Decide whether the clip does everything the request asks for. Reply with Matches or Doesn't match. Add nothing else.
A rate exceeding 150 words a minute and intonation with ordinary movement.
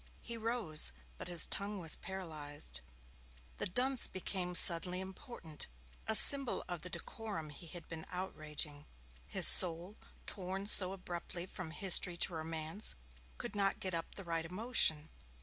Doesn't match